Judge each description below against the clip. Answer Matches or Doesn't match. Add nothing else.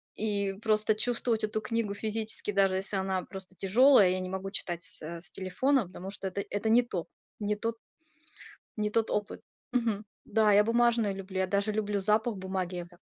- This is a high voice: Matches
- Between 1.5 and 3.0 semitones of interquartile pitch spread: Matches